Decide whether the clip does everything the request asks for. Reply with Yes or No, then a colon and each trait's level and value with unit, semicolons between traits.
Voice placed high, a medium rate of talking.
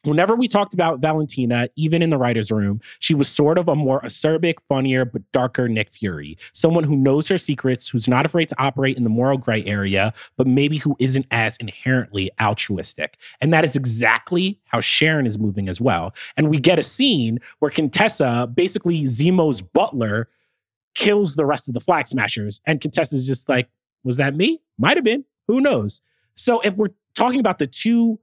No: medium, 140 Hz; average, 195 wpm